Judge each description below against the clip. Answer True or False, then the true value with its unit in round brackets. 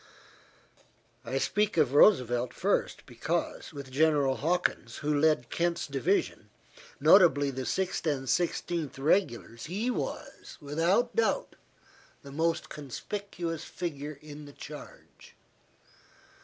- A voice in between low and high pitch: True (150 Hz)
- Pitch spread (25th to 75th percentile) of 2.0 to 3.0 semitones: False (4.1 semitones)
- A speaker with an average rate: False (110 wpm)